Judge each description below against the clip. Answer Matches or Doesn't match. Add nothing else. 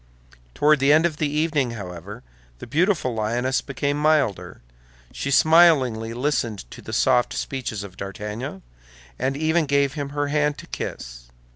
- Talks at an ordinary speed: Matches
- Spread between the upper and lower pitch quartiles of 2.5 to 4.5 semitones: Doesn't match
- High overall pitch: Doesn't match